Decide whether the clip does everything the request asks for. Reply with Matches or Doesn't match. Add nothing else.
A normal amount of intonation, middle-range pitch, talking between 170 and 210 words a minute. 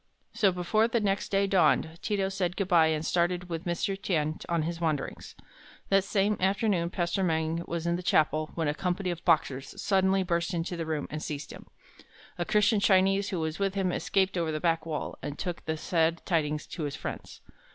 Matches